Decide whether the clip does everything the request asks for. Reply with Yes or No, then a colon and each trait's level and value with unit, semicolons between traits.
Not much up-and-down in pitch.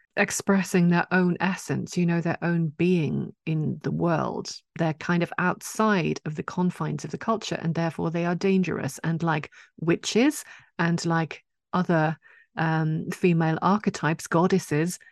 Yes: narrow, 2.3 semitones